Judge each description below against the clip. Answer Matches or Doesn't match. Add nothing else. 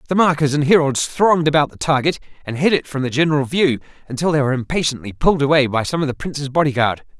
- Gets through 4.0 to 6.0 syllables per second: Doesn't match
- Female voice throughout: Doesn't match